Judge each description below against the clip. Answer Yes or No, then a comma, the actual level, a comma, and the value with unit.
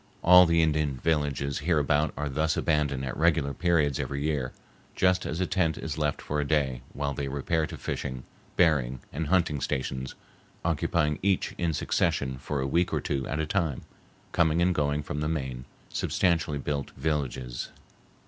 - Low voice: Yes, very low, 75 Hz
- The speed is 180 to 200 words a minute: No, average, 170 wpm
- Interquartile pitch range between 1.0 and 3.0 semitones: Yes, average, 2.7 semitones